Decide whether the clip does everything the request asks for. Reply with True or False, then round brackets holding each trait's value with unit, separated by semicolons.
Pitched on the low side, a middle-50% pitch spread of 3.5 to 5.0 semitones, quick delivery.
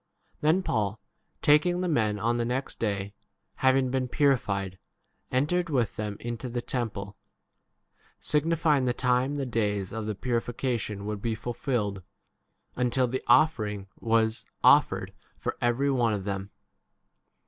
False (120 Hz; 4.1 semitones; 140 wpm)